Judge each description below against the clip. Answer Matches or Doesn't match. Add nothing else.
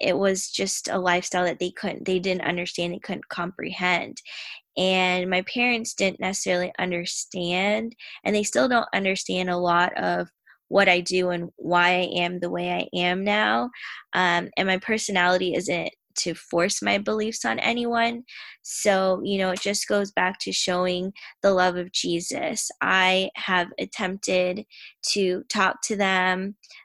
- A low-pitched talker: Doesn't match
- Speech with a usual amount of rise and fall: Doesn't match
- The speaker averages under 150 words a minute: Doesn't match